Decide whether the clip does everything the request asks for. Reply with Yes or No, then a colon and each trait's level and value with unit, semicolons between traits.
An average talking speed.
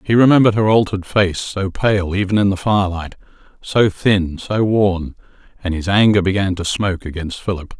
Yes: average, 175 wpm